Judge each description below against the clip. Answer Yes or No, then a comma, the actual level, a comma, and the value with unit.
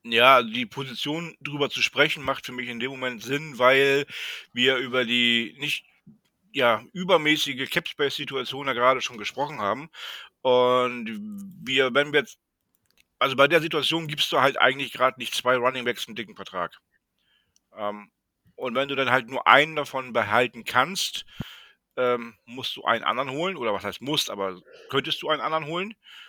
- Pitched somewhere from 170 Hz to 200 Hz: No, low, 135 Hz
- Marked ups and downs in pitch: No, average, 3.0 semitones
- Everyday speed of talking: Yes, average, 165 wpm